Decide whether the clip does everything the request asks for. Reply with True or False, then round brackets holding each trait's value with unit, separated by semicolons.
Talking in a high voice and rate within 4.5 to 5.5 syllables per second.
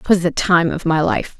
False (170 Hz; 4.7 syllables/s)